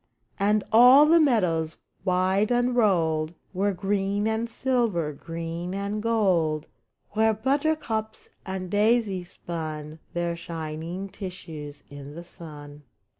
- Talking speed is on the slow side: Yes, slow, 110 wpm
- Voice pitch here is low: No, high, 190 Hz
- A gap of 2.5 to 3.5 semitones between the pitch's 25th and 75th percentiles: No, average, 5.0 semitones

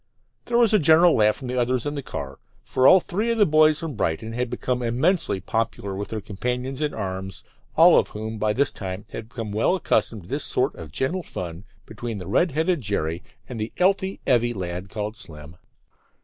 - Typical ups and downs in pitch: No, wide, 7.1 semitones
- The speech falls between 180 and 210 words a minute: Yes, fast, 205 wpm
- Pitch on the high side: No, low, 120 Hz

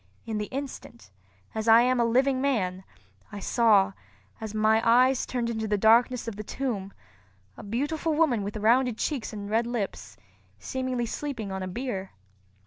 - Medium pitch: No, high, 230 Hz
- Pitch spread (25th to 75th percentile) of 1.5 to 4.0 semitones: Yes, average, 3.6 semitones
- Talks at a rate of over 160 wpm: Yes, average, 170 wpm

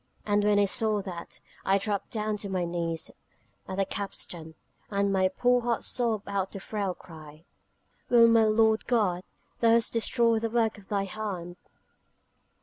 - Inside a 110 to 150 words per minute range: No, average, 160 wpm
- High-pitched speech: Yes, high, 205 Hz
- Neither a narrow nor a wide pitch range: Yes, average, 3.1 semitones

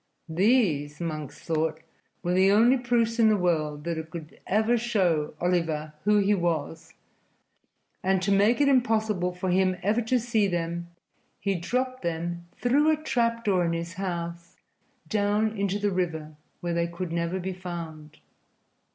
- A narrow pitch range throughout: No, average, 4.4 semitones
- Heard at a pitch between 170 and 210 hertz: Yes, medium, 185 Hz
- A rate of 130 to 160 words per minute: Yes, average, 155 wpm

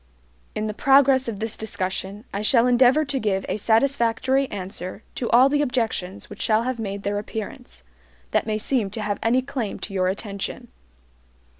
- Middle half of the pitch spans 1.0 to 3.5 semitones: No, average, 4.2 semitones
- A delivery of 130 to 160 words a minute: No, average, 175 wpm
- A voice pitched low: No, high, 220 Hz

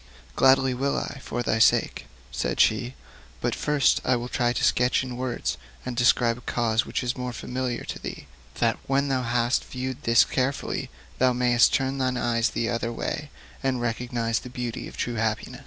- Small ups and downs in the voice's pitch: Yes, narrow, 1.6 semitones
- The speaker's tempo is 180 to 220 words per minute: Yes, average, 190 wpm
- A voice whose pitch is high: No, low, 125 Hz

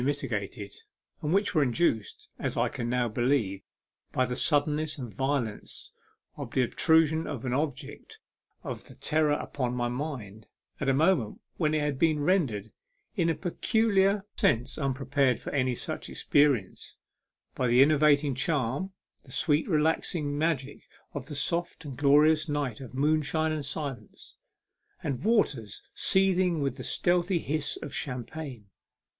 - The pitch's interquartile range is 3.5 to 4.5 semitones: Yes, average, 3.9 semitones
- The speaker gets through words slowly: No, average, 145 wpm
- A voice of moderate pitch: Yes, medium, 145 Hz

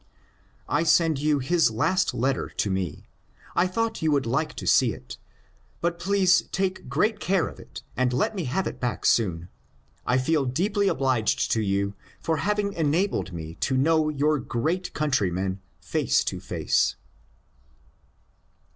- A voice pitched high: No, medium, 150 Hz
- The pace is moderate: Yes, average, 155 wpm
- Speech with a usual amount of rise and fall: No, wide, 7.0 semitones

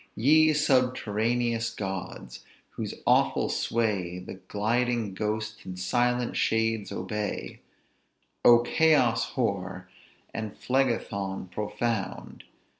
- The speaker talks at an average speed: No, slow, 90 wpm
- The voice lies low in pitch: Yes, low, 110 Hz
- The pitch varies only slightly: No, average, 3.8 semitones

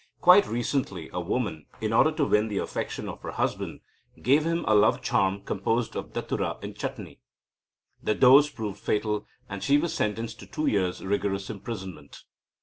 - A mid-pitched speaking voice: No, low, 110 Hz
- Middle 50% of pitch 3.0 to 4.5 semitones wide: No, wide, 5.4 semitones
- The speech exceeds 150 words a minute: Yes, average, 170 wpm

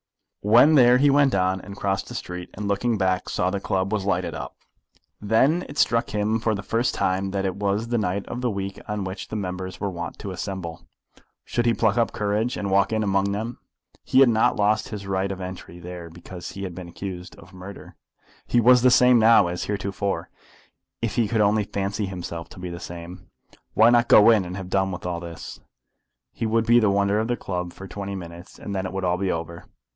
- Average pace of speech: No, fast, 225 wpm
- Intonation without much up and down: No, average, 3.1 semitones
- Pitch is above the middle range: No, low, 100 Hz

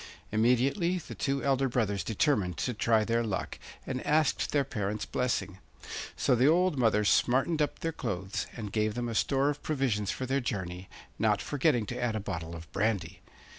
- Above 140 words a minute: Yes, average, 180 wpm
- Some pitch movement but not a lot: Yes, average, 4.8 semitones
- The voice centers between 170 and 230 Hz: No, low, 120 Hz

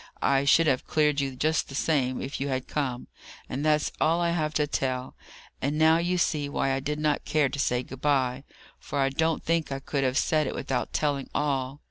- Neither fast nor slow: No, fast, 220 wpm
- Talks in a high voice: No, medium, 145 Hz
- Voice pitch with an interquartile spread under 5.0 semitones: Yes, narrow, 2.4 semitones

